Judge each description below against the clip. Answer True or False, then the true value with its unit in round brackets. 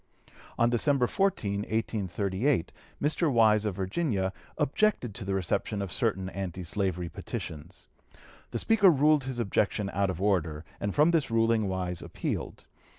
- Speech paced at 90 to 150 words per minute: True (145 wpm)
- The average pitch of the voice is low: True (105 Hz)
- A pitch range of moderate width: False (5.8 semitones)